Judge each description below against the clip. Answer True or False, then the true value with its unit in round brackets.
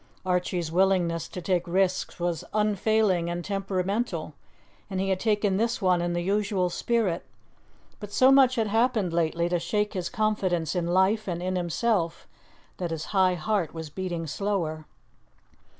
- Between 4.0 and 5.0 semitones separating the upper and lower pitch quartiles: False (3.2 semitones)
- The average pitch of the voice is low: False (185 Hz)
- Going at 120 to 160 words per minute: True (155 wpm)